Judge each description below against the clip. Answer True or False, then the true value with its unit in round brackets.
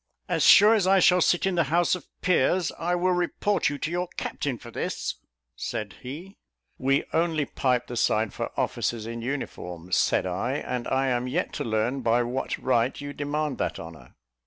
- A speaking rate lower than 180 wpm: False (190 wpm)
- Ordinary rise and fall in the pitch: False (6.5 semitones)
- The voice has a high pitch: False (135 Hz)